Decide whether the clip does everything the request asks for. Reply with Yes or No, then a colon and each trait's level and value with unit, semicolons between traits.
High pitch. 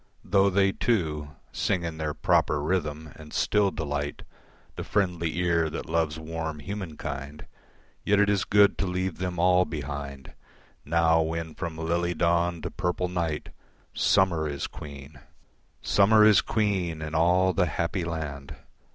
No: very low, 85 Hz